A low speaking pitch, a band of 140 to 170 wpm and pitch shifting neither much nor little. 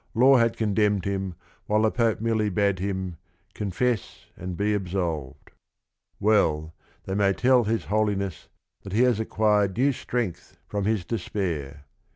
Yes: low, 105 Hz; average, 150 wpm; average, 3.0 semitones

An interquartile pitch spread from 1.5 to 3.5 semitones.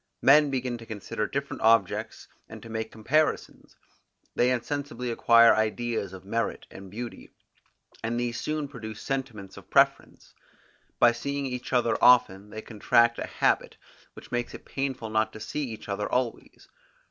Yes: average, 2.7 semitones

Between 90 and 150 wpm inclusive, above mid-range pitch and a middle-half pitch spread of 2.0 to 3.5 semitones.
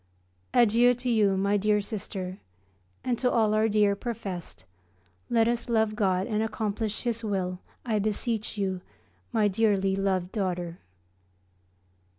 Yes: slow, 135 wpm; high, 210 Hz; average, 2.7 semitones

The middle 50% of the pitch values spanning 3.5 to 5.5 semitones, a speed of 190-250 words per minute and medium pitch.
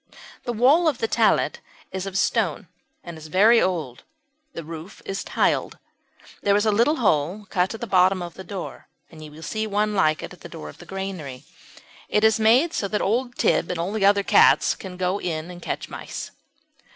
No: average, 4.0 semitones; fast, 205 wpm; high, 195 Hz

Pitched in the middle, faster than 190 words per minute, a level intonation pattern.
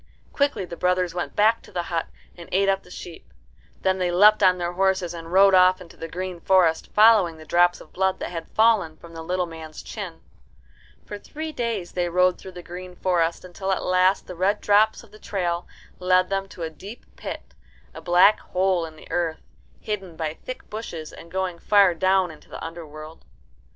Yes: medium, 180 Hz; average, 200 wpm; narrow, 2.3 semitones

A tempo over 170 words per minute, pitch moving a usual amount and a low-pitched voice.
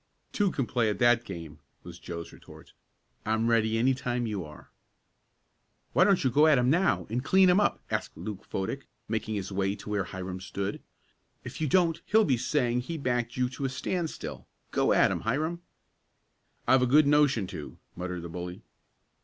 No: average, 185 wpm; wide, 6.6 semitones; low, 120 Hz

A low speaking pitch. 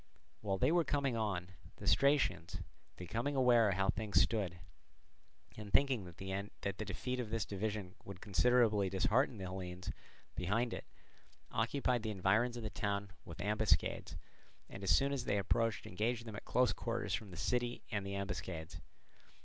Yes: low, 105 Hz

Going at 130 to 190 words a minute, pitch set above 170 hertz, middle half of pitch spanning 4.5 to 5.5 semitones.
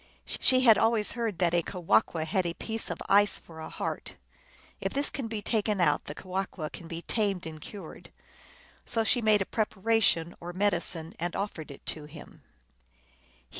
Yes: average, 175 wpm; high, 190 Hz; average, 4.8 semitones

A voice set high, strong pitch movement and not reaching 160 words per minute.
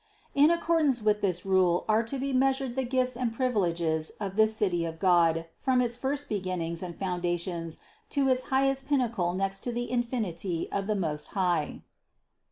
No: high, 210 Hz; wide, 6.6 semitones; average, 175 wpm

